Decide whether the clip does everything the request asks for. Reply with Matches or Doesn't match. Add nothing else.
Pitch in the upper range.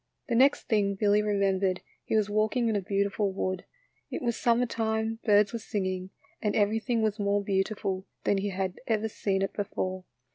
Matches